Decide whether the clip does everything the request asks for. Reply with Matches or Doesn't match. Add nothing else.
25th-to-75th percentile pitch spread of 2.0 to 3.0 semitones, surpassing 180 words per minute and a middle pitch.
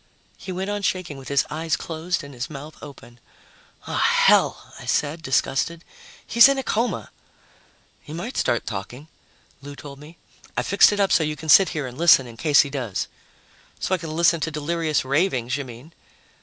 Doesn't match